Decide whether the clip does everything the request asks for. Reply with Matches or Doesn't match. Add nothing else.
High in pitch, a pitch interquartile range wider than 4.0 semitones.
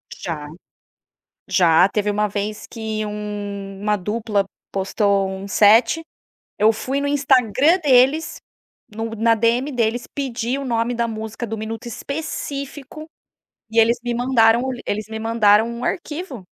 Doesn't match